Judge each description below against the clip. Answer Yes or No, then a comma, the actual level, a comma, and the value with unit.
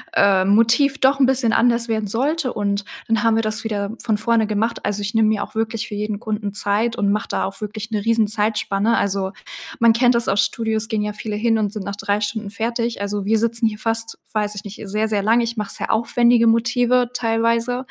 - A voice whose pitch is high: Yes, high, 220 Hz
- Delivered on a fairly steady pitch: Yes, narrow, 2.0 semitones